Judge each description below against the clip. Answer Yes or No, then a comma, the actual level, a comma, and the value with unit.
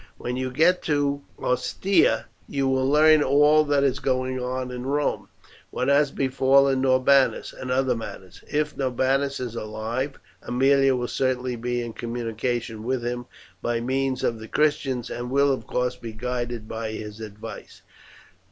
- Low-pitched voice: Yes, low, 130 Hz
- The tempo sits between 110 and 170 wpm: Yes, average, 155 wpm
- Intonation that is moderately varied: No, narrow, 2.3 semitones